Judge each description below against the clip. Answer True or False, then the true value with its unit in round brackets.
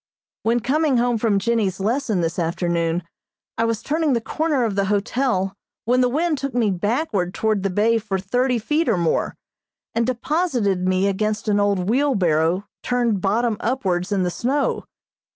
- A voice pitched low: False (220 Hz)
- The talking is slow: False (170 wpm)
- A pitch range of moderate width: True (4.5 semitones)